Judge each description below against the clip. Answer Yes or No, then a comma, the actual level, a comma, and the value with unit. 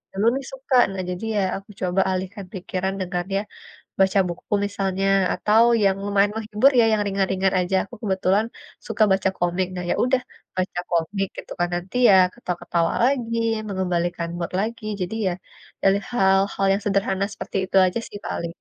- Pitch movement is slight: Yes, narrow, 2.1 semitones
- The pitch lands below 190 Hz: No, high, 195 Hz